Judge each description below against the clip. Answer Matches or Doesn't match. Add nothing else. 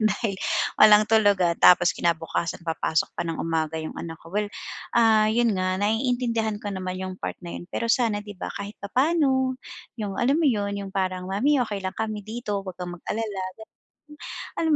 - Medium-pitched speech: Doesn't match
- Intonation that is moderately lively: Matches